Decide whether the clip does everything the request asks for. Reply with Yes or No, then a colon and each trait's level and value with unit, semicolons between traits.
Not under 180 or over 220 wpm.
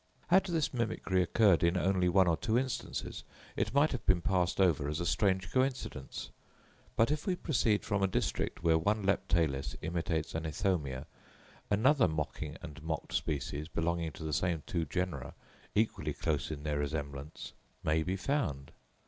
No: average, 165 wpm